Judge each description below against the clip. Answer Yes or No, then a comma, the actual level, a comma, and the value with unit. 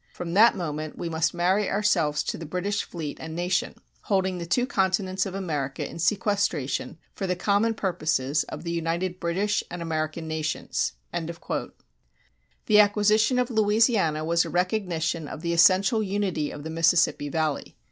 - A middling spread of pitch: Yes, average, 4.0 semitones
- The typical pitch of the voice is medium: Yes, medium, 175 Hz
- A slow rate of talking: No, average, 155 wpm